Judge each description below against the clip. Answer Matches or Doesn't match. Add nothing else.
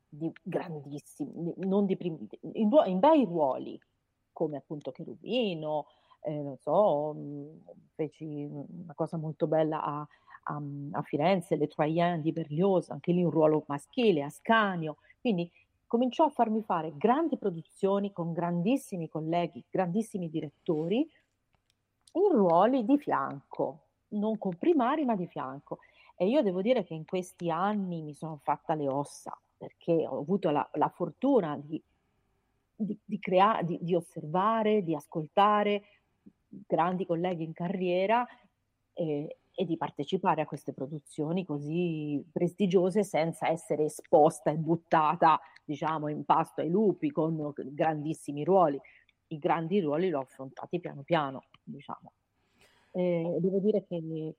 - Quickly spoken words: Doesn't match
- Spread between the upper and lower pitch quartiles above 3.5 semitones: Matches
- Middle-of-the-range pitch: Matches